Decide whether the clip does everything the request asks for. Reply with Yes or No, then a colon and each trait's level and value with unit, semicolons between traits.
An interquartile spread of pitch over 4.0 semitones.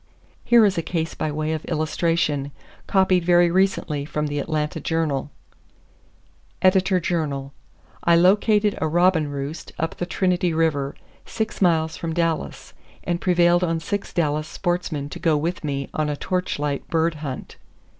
No: average, 2.9 semitones